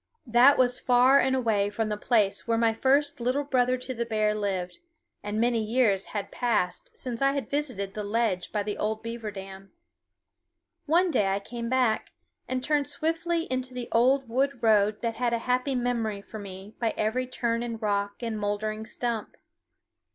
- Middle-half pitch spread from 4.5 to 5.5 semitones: No, average, 3.2 semitones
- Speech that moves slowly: No, average, 180 wpm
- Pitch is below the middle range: No, high, 230 Hz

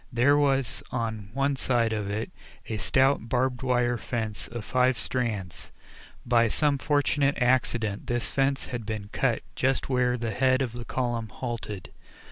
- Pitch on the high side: No, low, 120 Hz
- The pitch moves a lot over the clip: No, average, 2.8 semitones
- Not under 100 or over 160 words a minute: Yes, average, 155 wpm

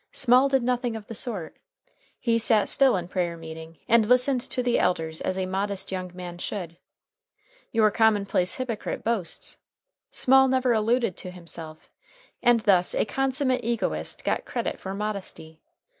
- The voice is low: No, high, 215 Hz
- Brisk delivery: No, average, 155 wpm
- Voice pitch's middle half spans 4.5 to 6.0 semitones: Yes, average, 5.2 semitones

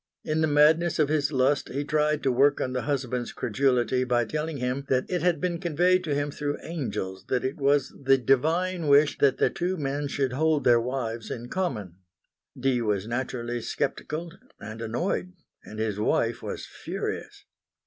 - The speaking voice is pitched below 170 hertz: Yes, medium, 140 Hz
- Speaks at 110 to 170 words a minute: No, average, 180 wpm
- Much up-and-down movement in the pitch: No, average, 3.9 semitones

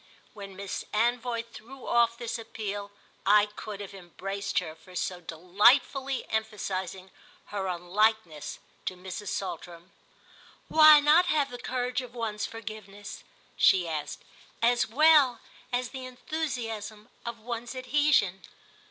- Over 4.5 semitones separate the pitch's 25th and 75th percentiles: No, average, 4.2 semitones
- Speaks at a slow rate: Yes, slow, 125 wpm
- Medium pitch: No, high, 220 Hz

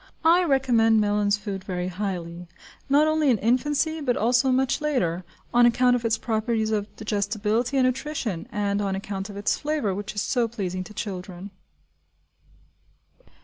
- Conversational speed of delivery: Yes, average, 155 wpm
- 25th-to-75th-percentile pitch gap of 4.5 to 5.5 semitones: No, average, 4.1 semitones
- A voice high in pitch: Yes, high, 220 Hz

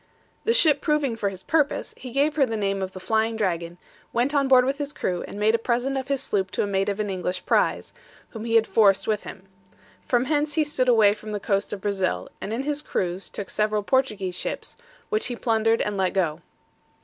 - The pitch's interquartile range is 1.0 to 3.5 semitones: No, average, 5.2 semitones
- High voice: Yes, high, 220 Hz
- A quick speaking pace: Yes, fast, 230 wpm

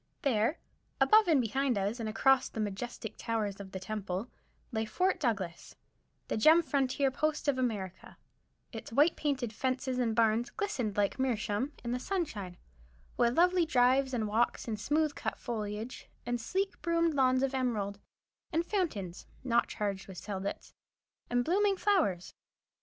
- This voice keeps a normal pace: Yes, average, 150 wpm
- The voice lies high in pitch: Yes, high, 245 Hz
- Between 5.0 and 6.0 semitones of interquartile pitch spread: Yes, average, 5.3 semitones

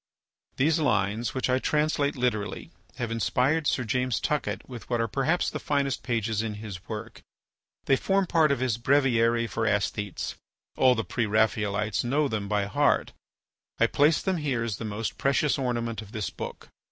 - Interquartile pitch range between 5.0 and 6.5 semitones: No, average, 4.2 semitones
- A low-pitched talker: Yes, low, 120 Hz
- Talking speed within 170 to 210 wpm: Yes, average, 175 wpm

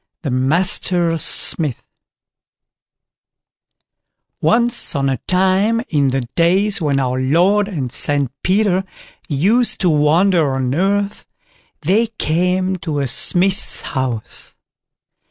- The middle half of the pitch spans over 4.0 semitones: Yes, wide, 5.6 semitones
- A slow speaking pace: Yes, slow, 105 wpm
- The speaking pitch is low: No, medium, 170 Hz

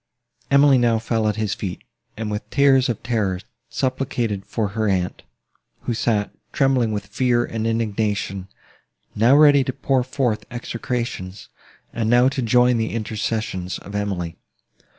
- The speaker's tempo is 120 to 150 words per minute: Yes, average, 145 wpm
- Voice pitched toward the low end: Yes, low, 115 Hz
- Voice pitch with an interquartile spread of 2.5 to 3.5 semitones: Yes, average, 3.2 semitones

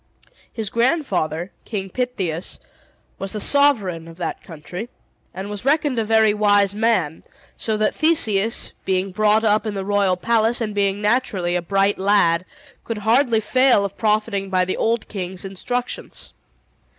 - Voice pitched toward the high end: Yes, high, 205 Hz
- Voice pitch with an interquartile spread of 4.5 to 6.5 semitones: No, average, 3.2 semitones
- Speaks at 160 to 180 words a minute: No, average, 150 wpm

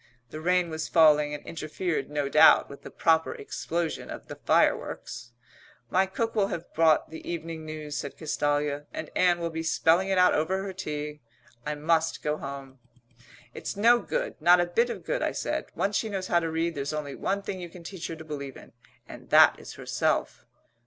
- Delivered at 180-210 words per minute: Yes, average, 200 wpm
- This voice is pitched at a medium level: Yes, medium, 165 Hz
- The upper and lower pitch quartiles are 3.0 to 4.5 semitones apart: Yes, average, 3.3 semitones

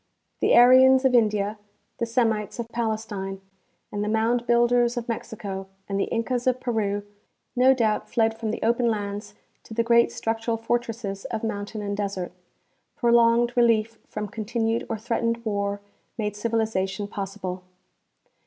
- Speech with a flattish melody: Yes, narrow, 2.3 semitones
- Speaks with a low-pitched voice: No, high, 225 Hz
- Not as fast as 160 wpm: Yes, average, 150 wpm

